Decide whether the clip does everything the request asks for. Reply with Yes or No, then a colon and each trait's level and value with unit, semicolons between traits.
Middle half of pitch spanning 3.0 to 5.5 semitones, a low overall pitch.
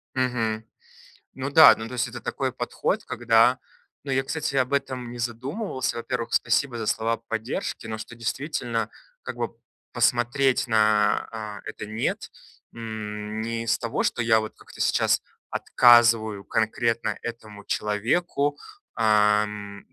No: narrow, 2.6 semitones; low, 115 Hz